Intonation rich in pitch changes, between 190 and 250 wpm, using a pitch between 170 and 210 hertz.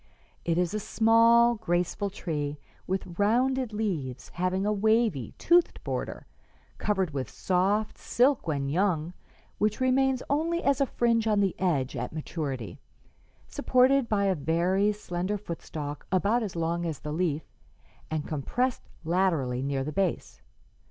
No: wide, 6.0 semitones; average, 145 wpm; high, 190 Hz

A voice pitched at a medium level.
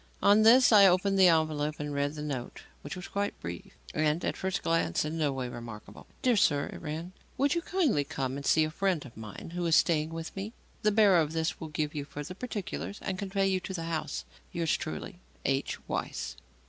Yes: medium, 165 Hz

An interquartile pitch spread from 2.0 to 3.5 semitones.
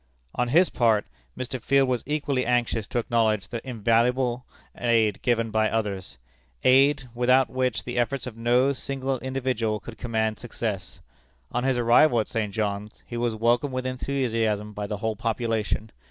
Yes: narrow, 2.6 semitones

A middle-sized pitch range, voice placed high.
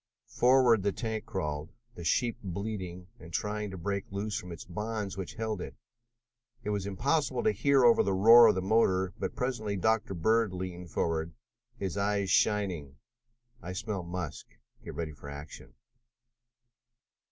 No: average, 3.6 semitones; low, 100 Hz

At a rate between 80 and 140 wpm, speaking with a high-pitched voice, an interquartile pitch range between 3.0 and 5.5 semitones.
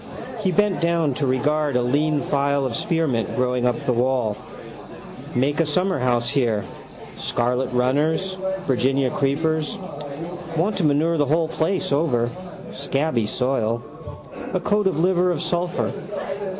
No: slow, 135 wpm; medium, 140 Hz; average, 4.7 semitones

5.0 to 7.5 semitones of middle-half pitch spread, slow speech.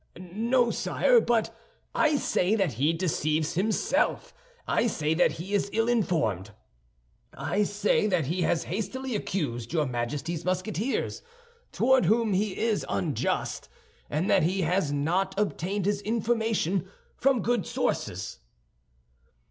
Yes: wide, 5.4 semitones; slow, 130 wpm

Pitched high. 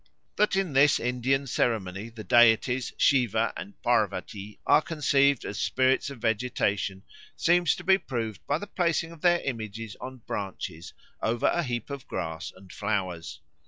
No: low, 120 Hz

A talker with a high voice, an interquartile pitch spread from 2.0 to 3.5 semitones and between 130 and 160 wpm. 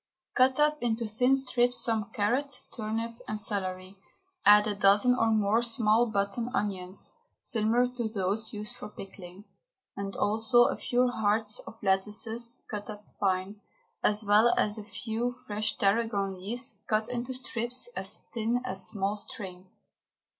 Yes: high, 215 Hz; average, 2.8 semitones; average, 145 wpm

